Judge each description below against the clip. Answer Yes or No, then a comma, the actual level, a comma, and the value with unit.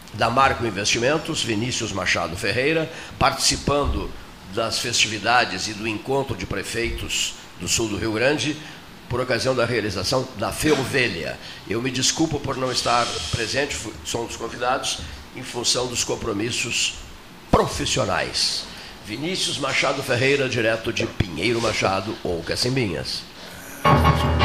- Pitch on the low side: Yes, low, 115 Hz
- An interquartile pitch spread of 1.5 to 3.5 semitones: No, average, 4.6 semitones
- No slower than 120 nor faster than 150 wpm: Yes, average, 125 wpm